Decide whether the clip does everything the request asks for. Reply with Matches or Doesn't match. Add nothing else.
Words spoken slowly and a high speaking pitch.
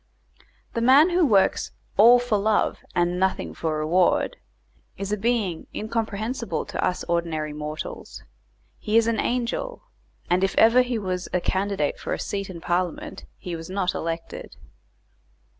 Doesn't match